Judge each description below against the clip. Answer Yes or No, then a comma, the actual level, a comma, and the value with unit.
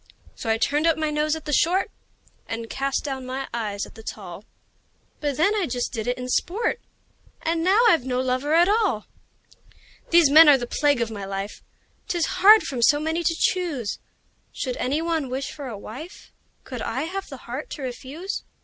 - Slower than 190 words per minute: No, average, 195 wpm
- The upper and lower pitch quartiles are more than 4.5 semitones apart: Yes, average, 5.0 semitones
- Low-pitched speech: No, very high, 285 Hz